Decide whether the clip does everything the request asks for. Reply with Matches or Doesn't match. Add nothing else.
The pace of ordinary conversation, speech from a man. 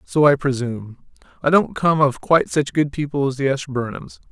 Matches